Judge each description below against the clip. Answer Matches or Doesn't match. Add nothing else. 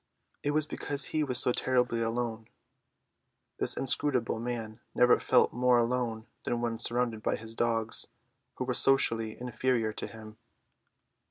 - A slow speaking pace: Doesn't match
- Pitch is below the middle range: Matches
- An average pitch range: Doesn't match